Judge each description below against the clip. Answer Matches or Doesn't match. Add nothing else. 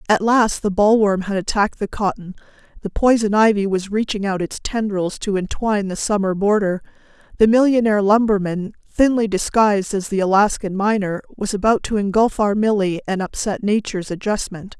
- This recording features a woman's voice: Matches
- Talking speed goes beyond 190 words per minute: Doesn't match